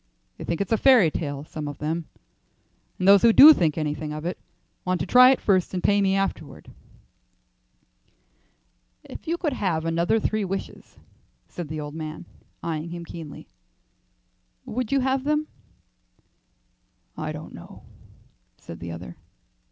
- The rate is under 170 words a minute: Yes, average, 150 wpm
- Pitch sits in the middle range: Yes, medium, 175 Hz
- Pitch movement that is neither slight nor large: No, wide, 5.9 semitones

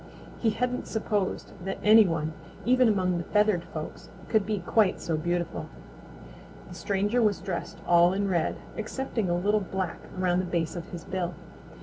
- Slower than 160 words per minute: No, average, 165 wpm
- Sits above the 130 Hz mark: Yes, high, 190 Hz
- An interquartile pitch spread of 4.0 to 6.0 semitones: No, average, 3.5 semitones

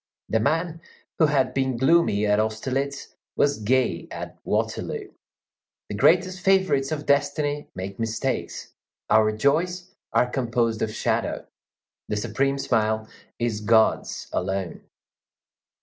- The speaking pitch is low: Yes, low, 130 Hz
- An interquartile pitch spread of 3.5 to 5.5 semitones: Yes, average, 5.0 semitones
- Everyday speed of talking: No, slow, 120 wpm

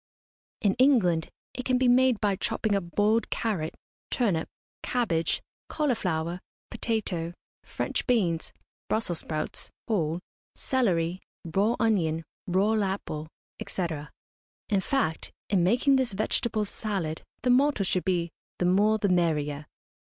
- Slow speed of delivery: Yes, slow, 125 wpm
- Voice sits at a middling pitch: No, high, 195 Hz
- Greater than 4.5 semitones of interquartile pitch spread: Yes, average, 5.3 semitones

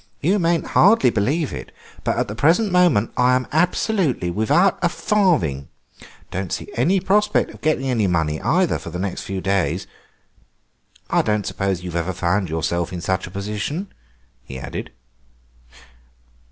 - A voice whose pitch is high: No, low, 110 Hz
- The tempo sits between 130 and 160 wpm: Yes, average, 155 wpm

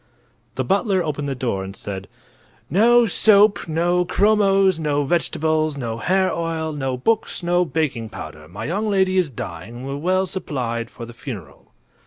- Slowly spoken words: No, average, 165 wpm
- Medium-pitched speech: Yes, medium, 155 Hz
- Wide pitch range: Yes, wide, 7.6 semitones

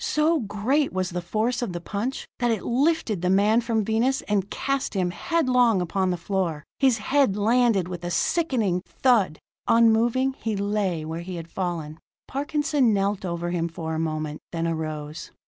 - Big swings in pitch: Yes, wide, 5.9 semitones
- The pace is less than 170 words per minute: No, average, 175 wpm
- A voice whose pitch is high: Yes, high, 200 Hz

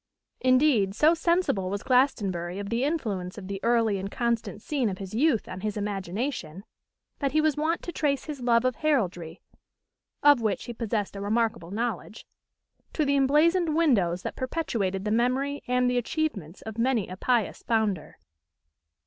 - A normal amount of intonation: No, wide, 5.9 semitones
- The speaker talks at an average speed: Yes, average, 165 wpm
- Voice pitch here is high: Yes, high, 230 Hz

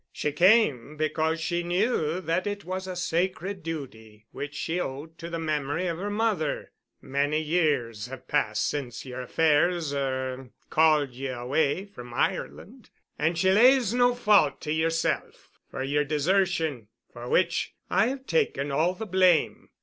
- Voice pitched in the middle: Yes, medium, 160 Hz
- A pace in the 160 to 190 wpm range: No, average, 150 wpm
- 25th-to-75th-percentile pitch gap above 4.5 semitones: Yes, average, 5.0 semitones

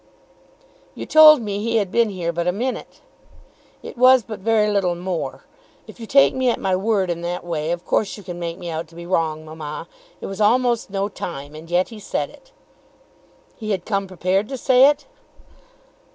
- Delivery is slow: No, average, 200 wpm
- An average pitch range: Yes, average, 4.8 semitones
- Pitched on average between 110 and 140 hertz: No, high, 195 Hz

